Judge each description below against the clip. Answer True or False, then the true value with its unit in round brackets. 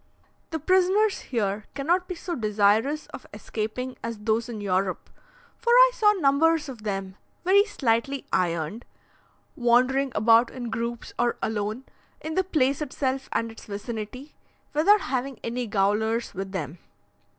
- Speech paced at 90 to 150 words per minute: True (140 wpm)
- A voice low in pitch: False (240 Hz)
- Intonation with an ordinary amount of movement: False (6.1 semitones)